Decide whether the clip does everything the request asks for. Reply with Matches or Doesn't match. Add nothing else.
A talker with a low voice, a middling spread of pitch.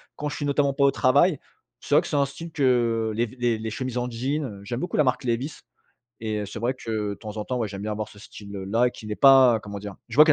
Matches